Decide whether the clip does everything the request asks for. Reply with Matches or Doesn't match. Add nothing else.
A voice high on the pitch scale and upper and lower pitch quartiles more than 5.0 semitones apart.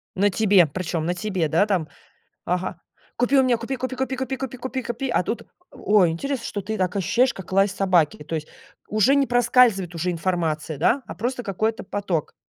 Matches